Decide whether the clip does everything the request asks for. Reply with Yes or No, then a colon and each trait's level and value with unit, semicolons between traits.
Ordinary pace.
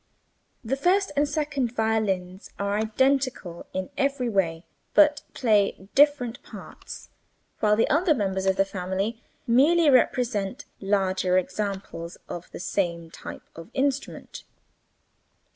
No: slow, 120 wpm